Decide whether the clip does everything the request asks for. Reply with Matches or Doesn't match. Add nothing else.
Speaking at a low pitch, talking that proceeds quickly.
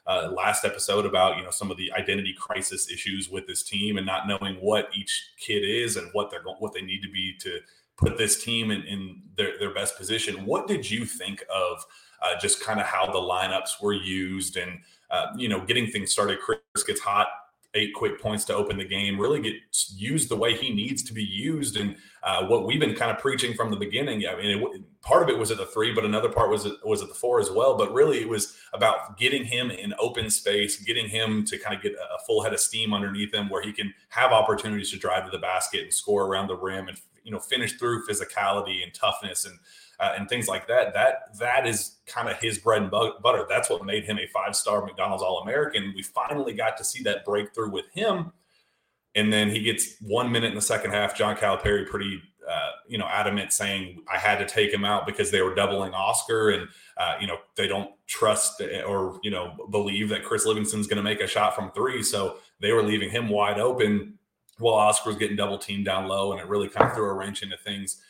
Matches